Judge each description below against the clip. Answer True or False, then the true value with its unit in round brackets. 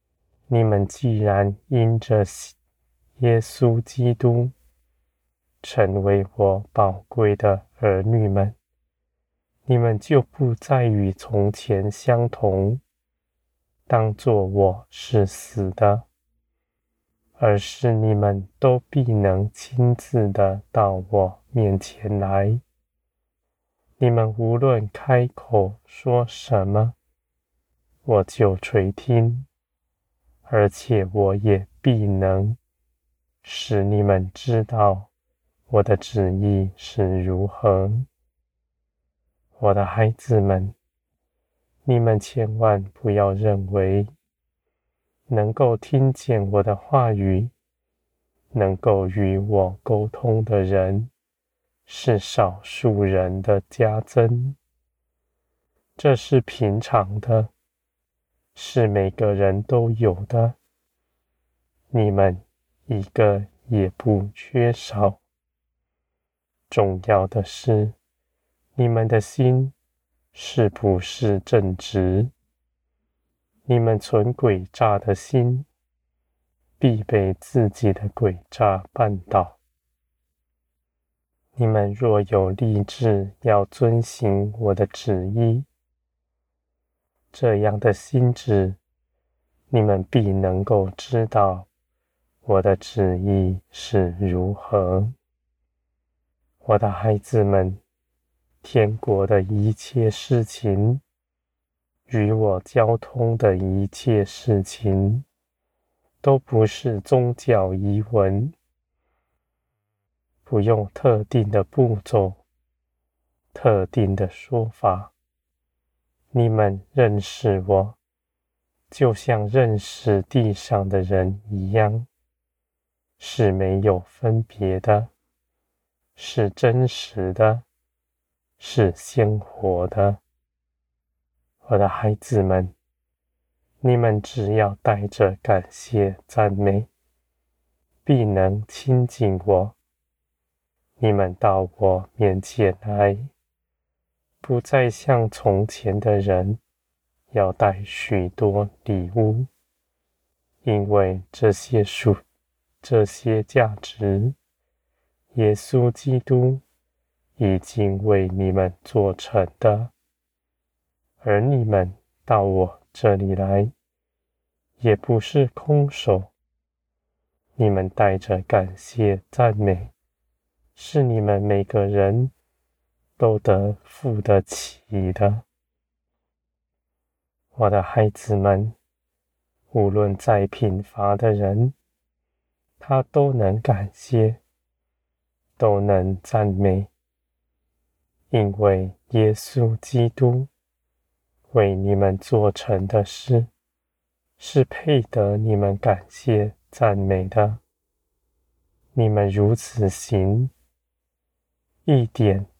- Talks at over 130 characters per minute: False (120 characters per minute)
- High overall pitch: False (100 Hz)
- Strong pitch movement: True (7.7 semitones)